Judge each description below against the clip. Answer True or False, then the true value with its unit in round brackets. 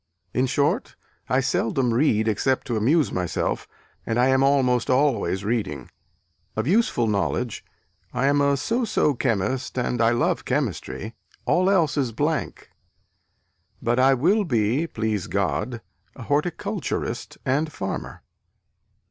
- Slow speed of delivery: True (130 wpm)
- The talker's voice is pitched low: True (130 Hz)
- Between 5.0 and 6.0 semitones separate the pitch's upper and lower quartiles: False (4.1 semitones)